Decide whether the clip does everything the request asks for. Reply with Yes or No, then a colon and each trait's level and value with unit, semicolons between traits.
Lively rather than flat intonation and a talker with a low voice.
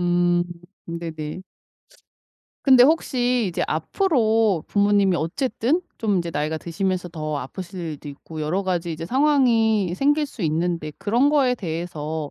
No: wide, 6.5 semitones; medium, 185 Hz